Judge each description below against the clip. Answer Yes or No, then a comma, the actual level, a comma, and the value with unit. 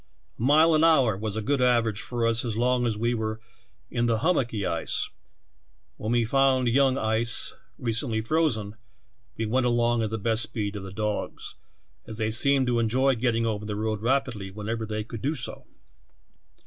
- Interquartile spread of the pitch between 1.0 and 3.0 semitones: Yes, narrow, 2.5 semitones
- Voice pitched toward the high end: No, low, 115 Hz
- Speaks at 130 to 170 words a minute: No, average, 185 wpm